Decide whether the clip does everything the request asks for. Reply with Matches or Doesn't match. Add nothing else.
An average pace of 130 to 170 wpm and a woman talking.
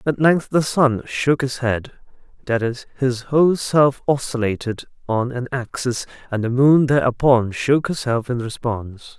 Doesn't match